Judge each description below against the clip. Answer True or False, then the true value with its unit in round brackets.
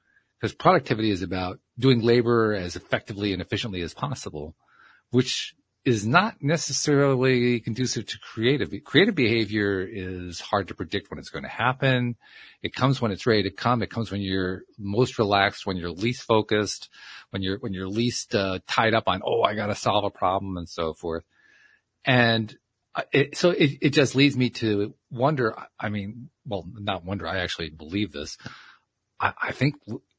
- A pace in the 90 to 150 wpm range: False (175 wpm)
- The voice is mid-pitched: False (110 Hz)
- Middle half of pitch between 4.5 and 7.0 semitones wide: True (4.8 semitones)